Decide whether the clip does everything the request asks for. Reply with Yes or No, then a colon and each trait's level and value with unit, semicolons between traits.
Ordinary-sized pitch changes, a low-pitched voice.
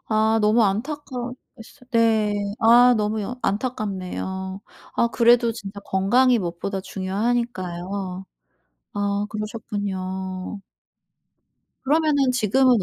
No: average, 3.9 semitones; high, 215 Hz